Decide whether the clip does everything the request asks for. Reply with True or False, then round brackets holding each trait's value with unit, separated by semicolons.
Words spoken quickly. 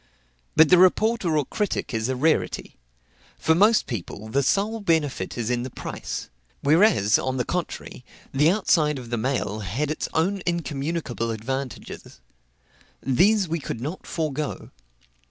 False (145 wpm)